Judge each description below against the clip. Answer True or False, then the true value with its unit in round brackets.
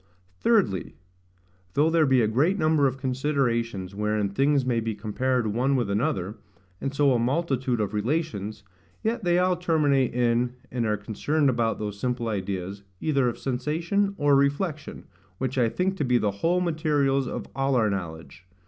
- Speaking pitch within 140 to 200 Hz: False (130 Hz)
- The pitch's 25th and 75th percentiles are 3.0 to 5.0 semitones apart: False (5.5 semitones)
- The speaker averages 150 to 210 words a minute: True (165 wpm)